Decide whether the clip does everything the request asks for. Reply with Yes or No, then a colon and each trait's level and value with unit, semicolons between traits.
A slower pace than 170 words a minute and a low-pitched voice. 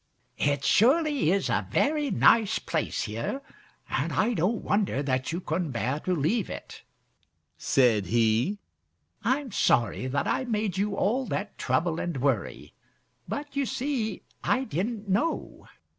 No: average, 145 wpm; high, 195 Hz